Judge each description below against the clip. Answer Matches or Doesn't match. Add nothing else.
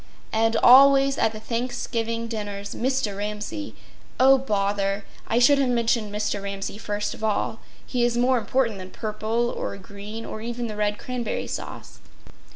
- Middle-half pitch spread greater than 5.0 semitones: Doesn't match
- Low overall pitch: Doesn't match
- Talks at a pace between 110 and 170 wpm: Matches